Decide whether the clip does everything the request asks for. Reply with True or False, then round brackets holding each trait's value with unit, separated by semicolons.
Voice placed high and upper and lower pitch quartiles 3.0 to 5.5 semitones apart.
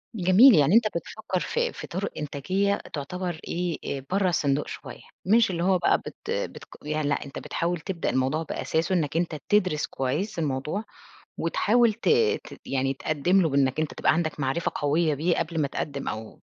False (165 Hz; 4.6 semitones)